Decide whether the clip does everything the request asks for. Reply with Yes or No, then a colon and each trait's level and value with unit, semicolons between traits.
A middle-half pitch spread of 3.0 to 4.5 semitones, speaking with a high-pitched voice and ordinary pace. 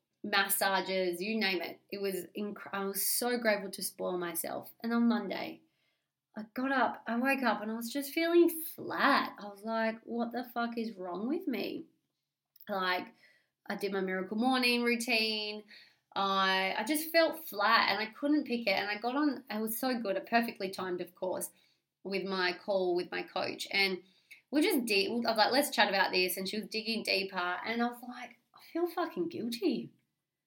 Yes: average, 4.0 semitones; high, 215 Hz; average, 195 wpm